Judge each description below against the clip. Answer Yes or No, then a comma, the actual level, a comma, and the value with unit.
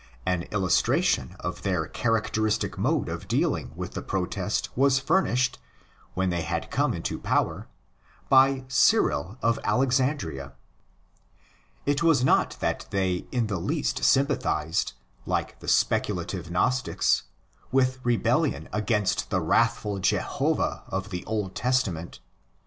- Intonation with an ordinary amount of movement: No, wide, 6.0 semitones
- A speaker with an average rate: No, slow, 125 wpm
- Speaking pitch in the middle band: No, low, 105 Hz